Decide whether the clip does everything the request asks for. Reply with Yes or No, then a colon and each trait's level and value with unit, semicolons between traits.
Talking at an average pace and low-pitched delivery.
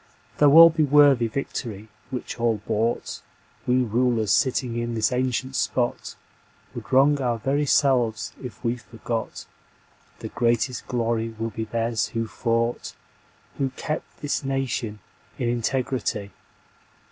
No: slow, 130 wpm; low, 120 Hz